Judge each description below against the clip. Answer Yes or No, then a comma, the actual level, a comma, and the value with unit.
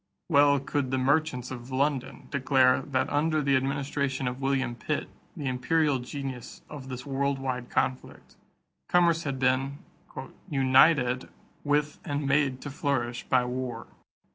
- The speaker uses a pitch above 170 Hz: No, low, 135 Hz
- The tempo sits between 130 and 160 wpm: Yes, average, 140 wpm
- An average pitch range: No, narrow, 1.9 semitones